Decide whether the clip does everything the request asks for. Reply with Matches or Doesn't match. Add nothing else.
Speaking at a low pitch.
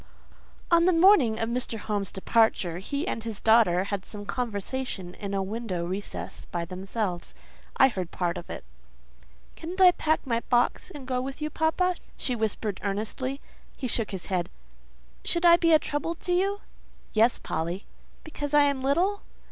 Doesn't match